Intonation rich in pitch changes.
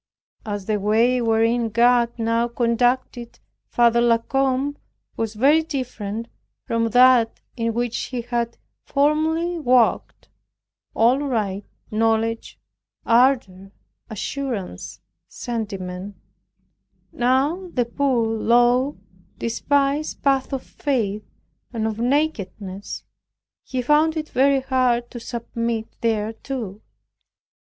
No: average, 3.0 semitones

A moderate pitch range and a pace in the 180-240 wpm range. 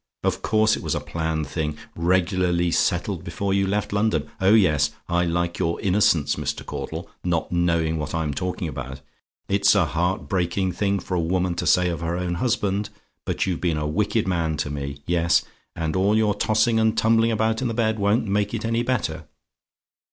Yes: average, 4.0 semitones; average, 195 wpm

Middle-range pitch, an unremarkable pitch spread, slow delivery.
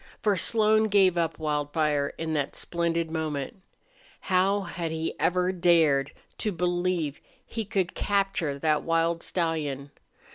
Yes: medium, 170 Hz; average, 3.1 semitones; slow, 130 wpm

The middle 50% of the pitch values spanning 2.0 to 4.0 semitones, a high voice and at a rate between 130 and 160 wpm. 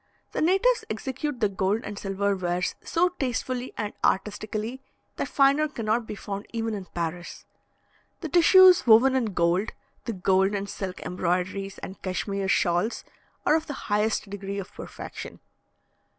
No: average, 5.0 semitones; high, 210 Hz; average, 150 wpm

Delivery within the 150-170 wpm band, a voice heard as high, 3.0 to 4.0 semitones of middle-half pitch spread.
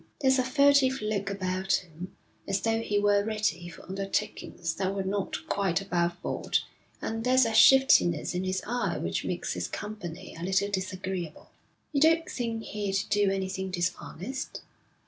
Yes: average, 160 wpm; high, 195 Hz; average, 3.3 semitones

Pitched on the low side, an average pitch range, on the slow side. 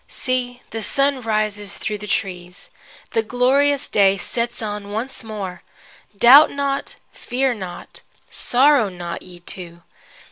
No: high, 220 Hz; average, 4.7 semitones; slow, 130 wpm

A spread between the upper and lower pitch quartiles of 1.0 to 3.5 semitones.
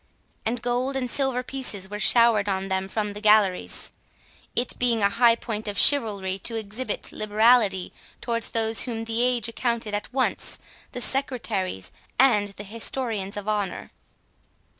Yes: average, 3.1 semitones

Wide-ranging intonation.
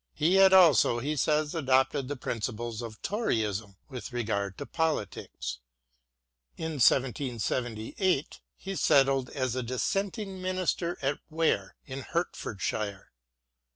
Yes: wide, 5.8 semitones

